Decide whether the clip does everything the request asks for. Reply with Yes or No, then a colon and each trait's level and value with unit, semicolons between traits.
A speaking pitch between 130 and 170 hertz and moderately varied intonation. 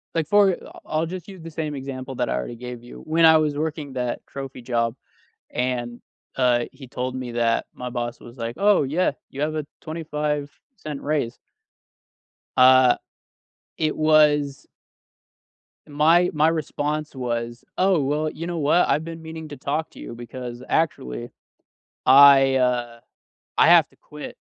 Yes: medium, 140 Hz; average, 4.0 semitones